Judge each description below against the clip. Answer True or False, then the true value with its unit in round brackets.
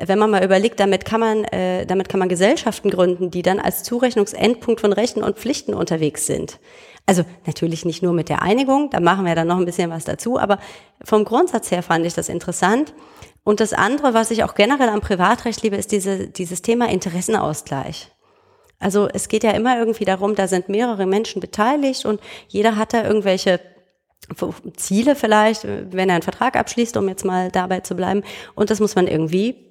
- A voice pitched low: False (200 Hz)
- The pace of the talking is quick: True (195 wpm)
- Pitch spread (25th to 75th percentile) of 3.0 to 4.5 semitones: True (3.6 semitones)